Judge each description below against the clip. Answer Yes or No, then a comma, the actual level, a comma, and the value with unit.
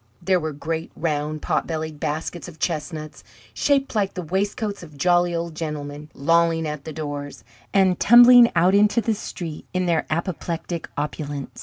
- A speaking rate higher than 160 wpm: No, average, 155 wpm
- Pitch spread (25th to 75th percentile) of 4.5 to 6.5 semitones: No, average, 3.2 semitones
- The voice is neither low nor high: Yes, medium, 165 Hz